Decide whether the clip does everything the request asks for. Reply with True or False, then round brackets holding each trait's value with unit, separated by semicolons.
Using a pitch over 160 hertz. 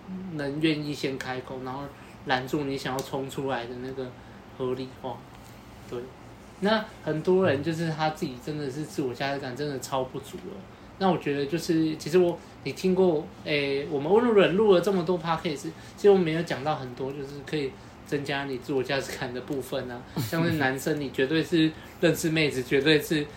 False (145 Hz)